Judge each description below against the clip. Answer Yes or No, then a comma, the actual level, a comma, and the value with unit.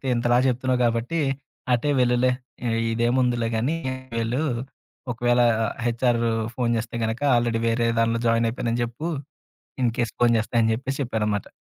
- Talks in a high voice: No, low, 120 Hz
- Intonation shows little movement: Yes, narrow, 1.2 semitones